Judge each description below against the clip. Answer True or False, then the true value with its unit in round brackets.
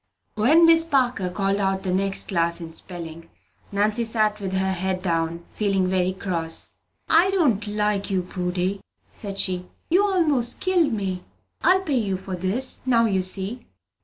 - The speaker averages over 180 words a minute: False (165 wpm)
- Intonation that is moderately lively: True (4.5 semitones)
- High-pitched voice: True (195 Hz)